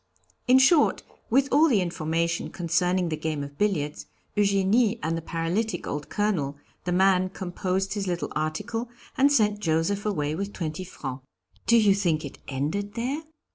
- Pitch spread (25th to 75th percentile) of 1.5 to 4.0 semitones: No, average, 4.6 semitones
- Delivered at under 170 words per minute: Yes, average, 160 wpm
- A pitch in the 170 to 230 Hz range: Yes, medium, 185 Hz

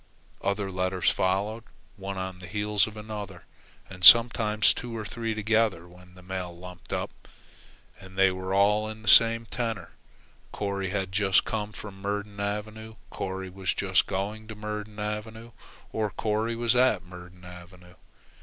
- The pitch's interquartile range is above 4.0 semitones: No, narrow, 2.5 semitones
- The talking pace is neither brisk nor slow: Yes, average, 155 wpm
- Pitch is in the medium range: No, low, 100 Hz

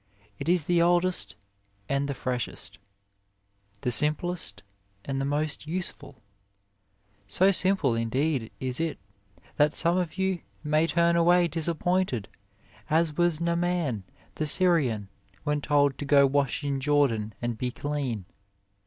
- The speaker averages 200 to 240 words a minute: No, slow, 135 wpm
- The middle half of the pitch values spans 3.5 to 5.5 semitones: Yes, average, 4.4 semitones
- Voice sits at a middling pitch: Yes, medium, 150 Hz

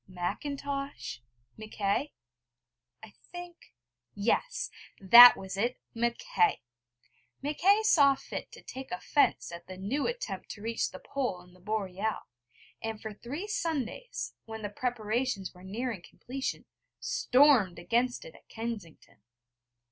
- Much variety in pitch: Yes, wide, 6.2 semitones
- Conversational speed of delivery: No, slow, 125 wpm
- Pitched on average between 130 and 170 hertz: No, high, 235 Hz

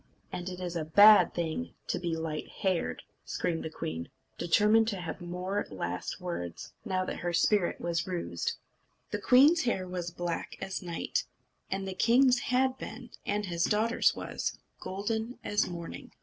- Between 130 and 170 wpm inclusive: Yes, average, 155 wpm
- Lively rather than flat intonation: No, average, 3.8 semitones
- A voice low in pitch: No, medium, 185 Hz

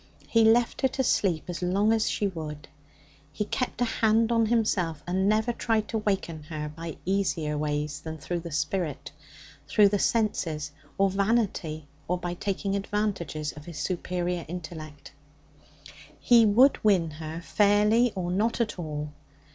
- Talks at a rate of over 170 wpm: No, average, 155 wpm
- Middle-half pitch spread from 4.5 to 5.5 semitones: Yes, average, 5.2 semitones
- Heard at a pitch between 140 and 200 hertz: Yes, medium, 185 Hz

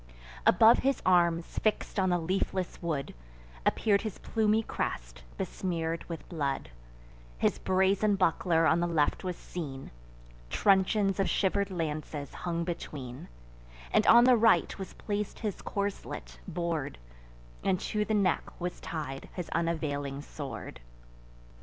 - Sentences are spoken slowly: Yes, slow, 130 wpm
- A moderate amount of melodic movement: Yes, average, 4.3 semitones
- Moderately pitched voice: Yes, medium, 175 Hz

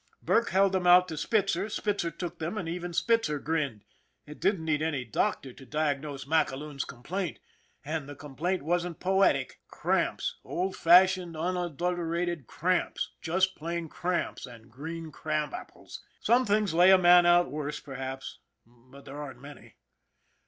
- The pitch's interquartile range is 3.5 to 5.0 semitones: Yes, average, 3.8 semitones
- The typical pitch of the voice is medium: Yes, medium, 165 Hz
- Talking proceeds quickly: No, average, 150 wpm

